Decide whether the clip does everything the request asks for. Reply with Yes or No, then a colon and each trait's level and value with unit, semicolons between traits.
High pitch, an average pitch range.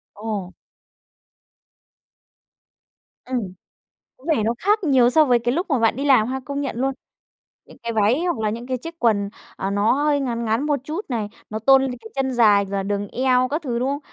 Yes: high, 245 Hz; average, 4.2 semitones